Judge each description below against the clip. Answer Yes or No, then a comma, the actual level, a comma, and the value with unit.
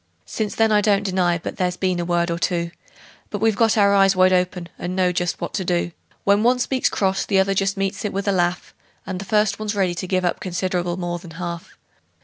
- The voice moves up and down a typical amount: No, narrow, 2.3 semitones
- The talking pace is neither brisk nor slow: No, fast, 240 wpm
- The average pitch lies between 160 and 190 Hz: Yes, medium, 185 Hz